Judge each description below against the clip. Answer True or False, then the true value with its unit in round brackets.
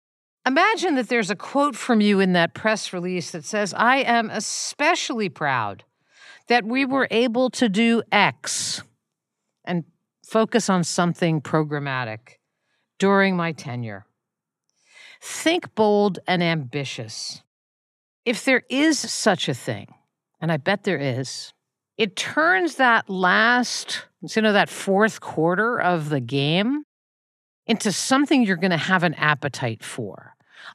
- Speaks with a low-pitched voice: False (195 Hz)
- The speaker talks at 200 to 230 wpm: False (135 wpm)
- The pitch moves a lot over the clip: True (7.2 semitones)